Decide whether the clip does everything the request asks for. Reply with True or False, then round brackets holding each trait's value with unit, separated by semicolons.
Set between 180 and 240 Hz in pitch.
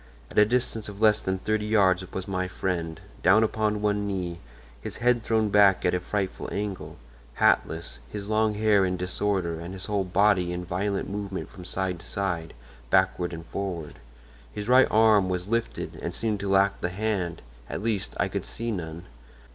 False (100 Hz)